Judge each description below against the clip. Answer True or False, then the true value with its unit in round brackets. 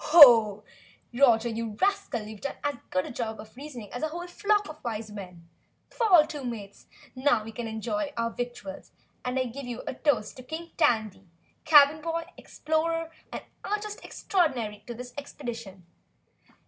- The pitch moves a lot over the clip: True (6.1 semitones)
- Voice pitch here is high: True (250 Hz)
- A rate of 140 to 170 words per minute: True (160 wpm)